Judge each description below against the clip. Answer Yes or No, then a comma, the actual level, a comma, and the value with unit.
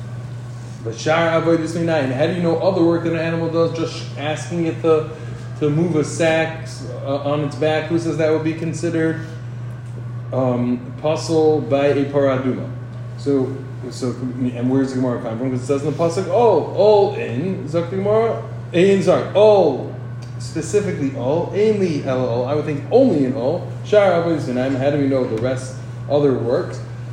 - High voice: No, medium, 140 Hz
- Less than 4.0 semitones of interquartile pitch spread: No, average, 4.7 semitones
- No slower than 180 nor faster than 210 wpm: No, average, 165 wpm